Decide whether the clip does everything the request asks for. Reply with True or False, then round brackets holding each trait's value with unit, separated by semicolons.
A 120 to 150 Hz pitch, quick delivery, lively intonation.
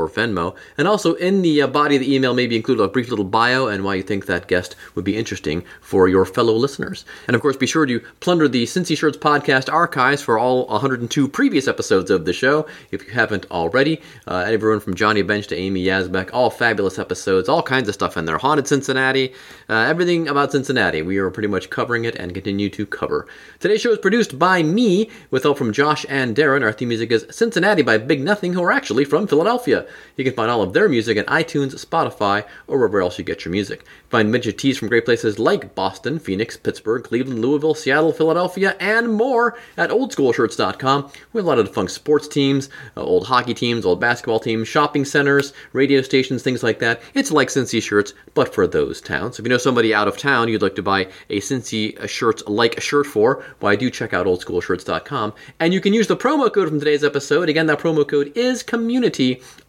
True (135 Hz; 215 wpm; 6.1 semitones)